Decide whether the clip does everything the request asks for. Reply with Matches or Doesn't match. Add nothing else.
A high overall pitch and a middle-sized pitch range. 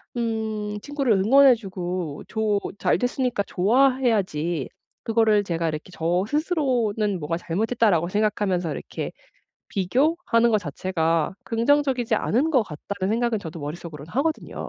Doesn't match